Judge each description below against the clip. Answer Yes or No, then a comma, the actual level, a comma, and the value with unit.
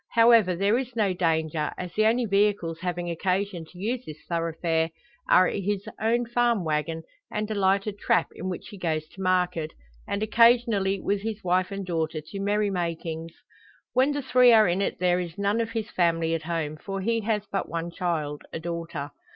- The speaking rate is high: No, average, 190 wpm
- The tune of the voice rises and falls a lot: No, average, 4.1 semitones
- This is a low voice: No, medium, 185 Hz